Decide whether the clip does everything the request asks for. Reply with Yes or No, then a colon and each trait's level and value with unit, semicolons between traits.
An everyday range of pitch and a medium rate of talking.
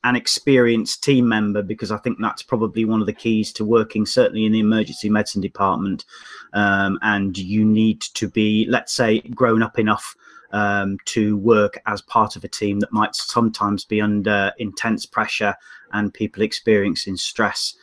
No: narrow, 1.4 semitones; average, 170 wpm